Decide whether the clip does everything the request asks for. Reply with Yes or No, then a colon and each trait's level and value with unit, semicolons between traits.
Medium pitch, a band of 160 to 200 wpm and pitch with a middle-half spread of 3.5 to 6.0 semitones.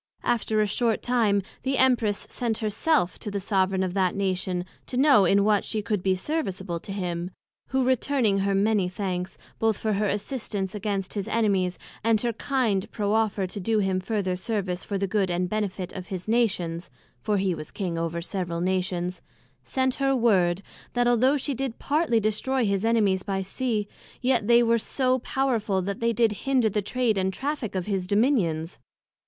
No: high, 205 Hz; average, 185 wpm; average, 3.8 semitones